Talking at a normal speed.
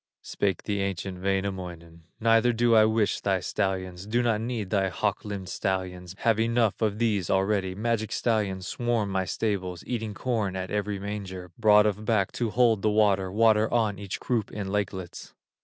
Yes: average, 175 wpm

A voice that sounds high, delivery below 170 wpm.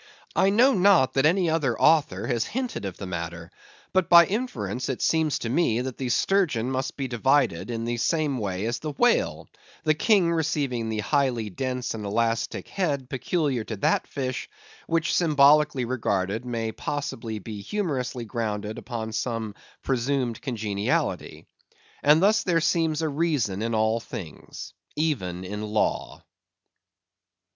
No: low, 130 Hz; average, 150 wpm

